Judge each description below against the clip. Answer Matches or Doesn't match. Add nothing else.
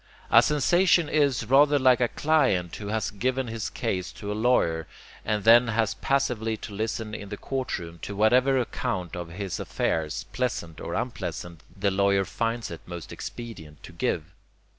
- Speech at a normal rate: Matches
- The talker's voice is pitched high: Doesn't match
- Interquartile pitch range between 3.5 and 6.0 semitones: Matches